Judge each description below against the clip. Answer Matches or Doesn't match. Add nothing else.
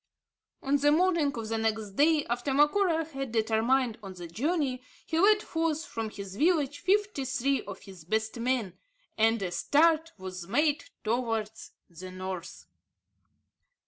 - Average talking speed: Matches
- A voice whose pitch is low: Doesn't match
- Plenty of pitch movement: Matches